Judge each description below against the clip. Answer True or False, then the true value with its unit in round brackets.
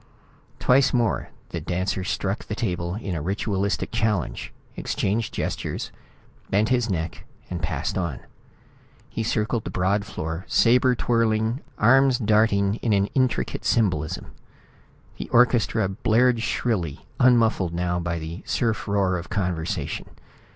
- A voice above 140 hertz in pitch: False (105 Hz)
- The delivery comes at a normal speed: False (125 wpm)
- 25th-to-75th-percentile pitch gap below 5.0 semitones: True (4.4 semitones)